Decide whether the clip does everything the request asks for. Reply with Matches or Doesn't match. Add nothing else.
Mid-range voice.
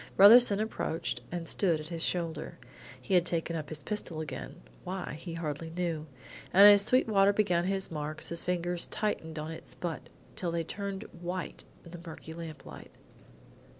Matches